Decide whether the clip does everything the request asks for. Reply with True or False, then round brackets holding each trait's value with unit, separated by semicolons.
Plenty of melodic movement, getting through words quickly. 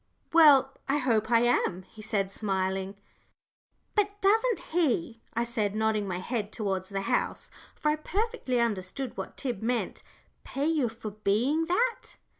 False (6.7 semitones; 150 wpm)